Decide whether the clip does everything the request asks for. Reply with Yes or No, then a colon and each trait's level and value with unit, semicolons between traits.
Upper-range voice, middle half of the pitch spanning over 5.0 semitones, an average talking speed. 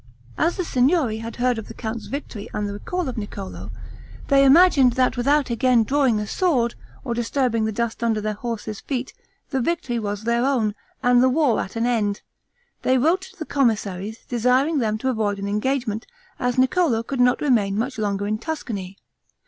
No: high, 240 Hz; average, 3.7 semitones; average, 190 wpm